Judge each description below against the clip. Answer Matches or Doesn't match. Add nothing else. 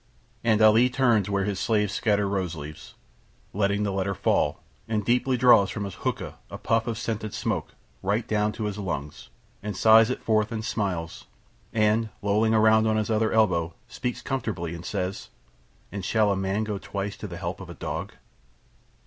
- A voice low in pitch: Matches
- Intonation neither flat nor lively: Doesn't match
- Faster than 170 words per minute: Matches